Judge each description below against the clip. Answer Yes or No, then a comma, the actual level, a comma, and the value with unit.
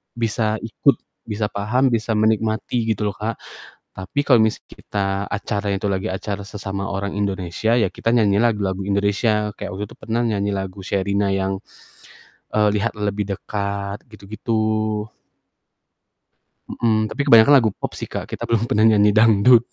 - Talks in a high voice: No, low, 105 Hz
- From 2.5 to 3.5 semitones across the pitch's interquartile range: No, narrow, 1.8 semitones